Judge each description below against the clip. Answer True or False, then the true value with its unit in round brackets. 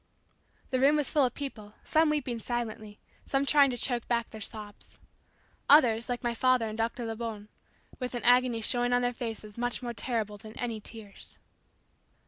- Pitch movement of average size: False (2.3 semitones)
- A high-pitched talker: True (240 Hz)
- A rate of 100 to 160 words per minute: False (175 wpm)